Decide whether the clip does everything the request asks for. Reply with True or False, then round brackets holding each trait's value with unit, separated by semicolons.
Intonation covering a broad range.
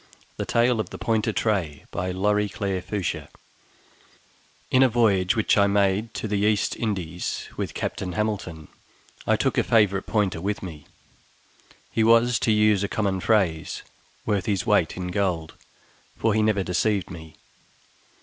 False (2.9 semitones)